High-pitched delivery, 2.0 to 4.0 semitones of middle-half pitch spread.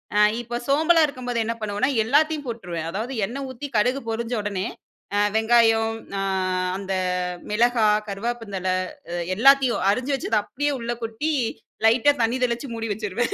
Yes: high, 235 Hz; average, 3.4 semitones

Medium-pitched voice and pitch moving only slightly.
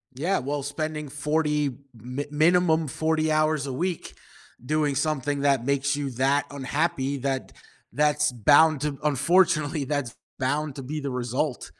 Yes: medium, 145 Hz; narrow, 2.2 semitones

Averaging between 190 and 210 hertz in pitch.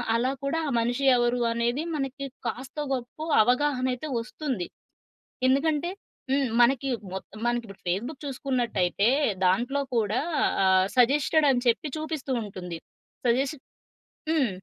No: very high, 250 Hz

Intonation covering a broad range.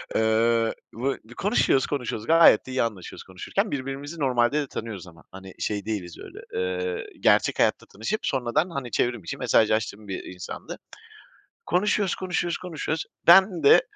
Yes: wide, 7.1 semitones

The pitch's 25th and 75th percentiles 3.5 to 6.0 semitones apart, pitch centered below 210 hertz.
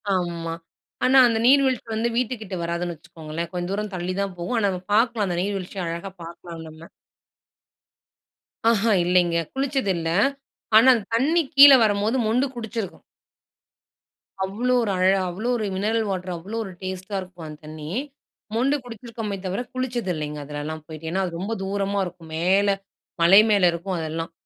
Yes: average, 4.7 semitones; high, 190 Hz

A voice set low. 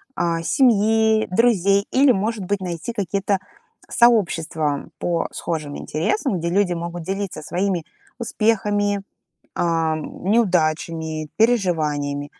No: medium, 185 Hz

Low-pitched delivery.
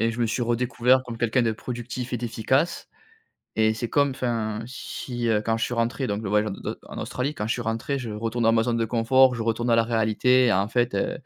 Yes: low, 115 Hz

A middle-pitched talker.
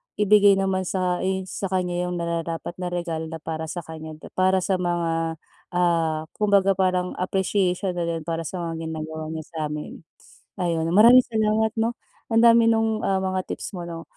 Yes: medium, 180 Hz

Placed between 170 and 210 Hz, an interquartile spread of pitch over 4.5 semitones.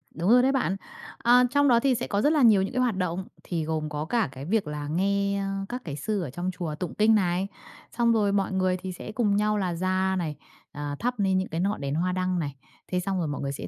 No: high, 190 Hz; average, 4.2 semitones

